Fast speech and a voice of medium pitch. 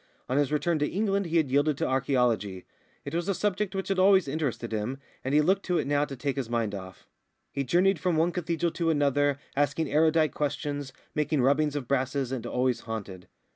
Yes: fast, 210 wpm; medium, 145 Hz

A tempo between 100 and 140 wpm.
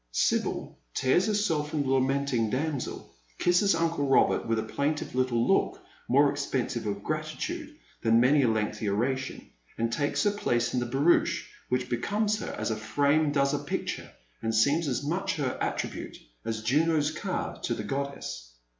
No: average, 165 wpm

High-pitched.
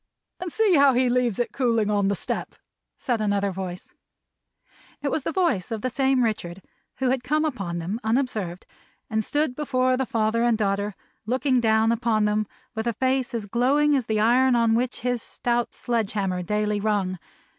Yes: high, 230 Hz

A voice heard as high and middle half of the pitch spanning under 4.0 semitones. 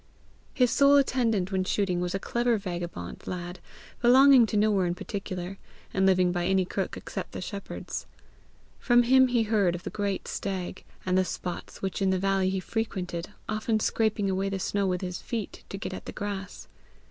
Yes: high, 195 Hz; average, 3.1 semitones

